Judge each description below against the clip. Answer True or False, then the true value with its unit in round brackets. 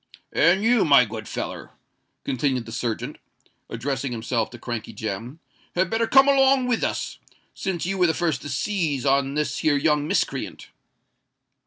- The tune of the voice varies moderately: False (7.7 semitones)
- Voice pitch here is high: False (145 Hz)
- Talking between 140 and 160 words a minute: True (155 wpm)